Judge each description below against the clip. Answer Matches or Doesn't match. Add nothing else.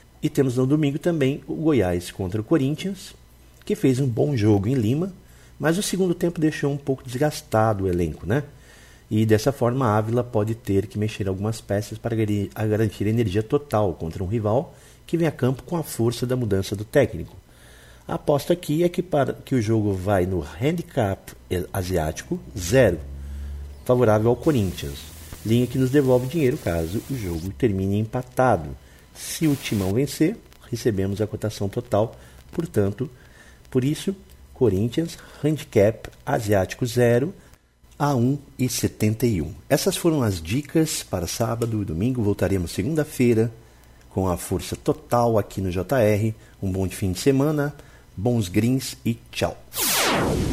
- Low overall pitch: Matches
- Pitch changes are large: Matches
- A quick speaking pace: Doesn't match